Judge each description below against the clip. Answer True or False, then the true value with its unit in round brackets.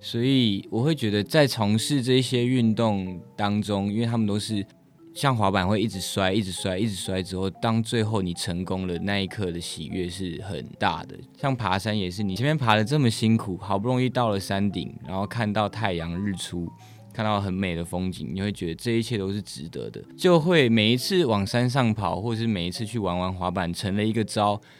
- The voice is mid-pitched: False (105 Hz)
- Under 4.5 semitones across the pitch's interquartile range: True (3.5 semitones)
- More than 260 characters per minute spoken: True (305 characters per minute)